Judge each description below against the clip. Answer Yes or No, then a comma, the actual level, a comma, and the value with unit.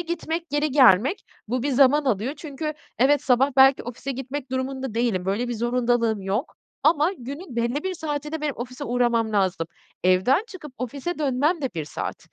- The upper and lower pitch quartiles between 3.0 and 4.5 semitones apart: Yes, average, 3.8 semitones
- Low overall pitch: No, very high, 265 Hz